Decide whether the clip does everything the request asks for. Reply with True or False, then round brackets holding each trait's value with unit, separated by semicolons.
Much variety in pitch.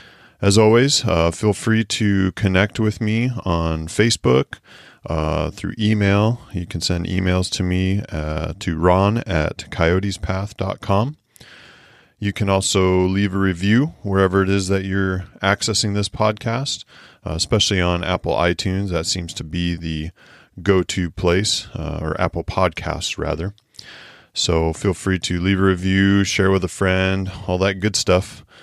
False (2.6 semitones)